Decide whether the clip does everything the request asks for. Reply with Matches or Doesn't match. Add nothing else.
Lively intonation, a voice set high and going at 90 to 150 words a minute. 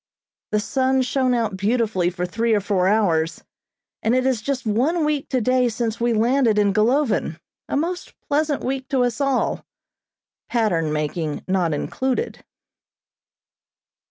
Doesn't match